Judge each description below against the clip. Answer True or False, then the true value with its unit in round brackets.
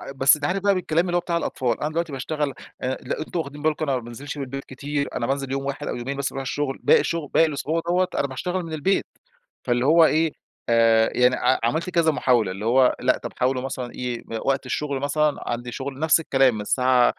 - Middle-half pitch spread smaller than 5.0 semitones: True (3.6 semitones)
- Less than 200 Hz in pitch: True (140 Hz)